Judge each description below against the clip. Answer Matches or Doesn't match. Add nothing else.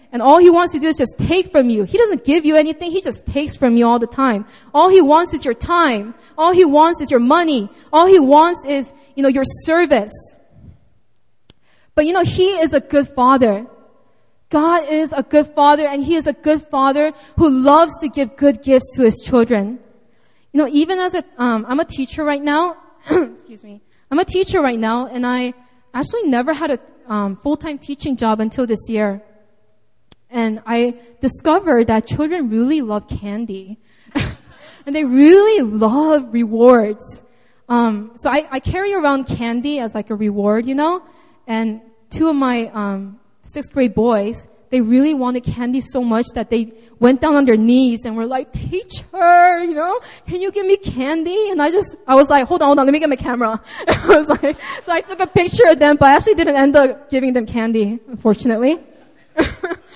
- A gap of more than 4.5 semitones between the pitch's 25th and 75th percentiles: Matches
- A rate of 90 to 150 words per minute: Doesn't match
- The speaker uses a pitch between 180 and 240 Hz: Doesn't match